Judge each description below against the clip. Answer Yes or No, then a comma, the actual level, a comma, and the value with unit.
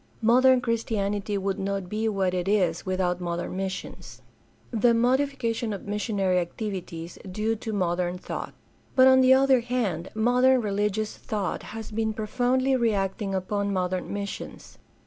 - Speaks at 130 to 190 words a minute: Yes, average, 140 wpm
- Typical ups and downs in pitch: Yes, average, 3.8 semitones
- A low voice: No, high, 210 Hz